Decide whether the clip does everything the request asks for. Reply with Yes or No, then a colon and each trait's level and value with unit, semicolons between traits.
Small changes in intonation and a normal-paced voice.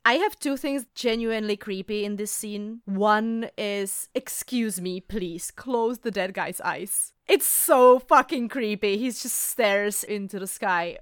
No: average, 3.4 semitones; average, 160 wpm